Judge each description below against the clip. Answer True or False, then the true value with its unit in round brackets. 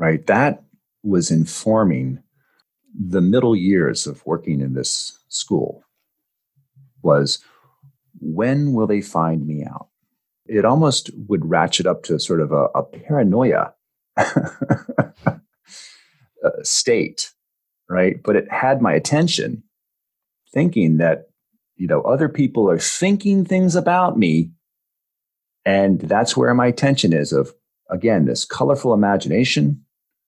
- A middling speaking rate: False (115 wpm)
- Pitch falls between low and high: False (105 Hz)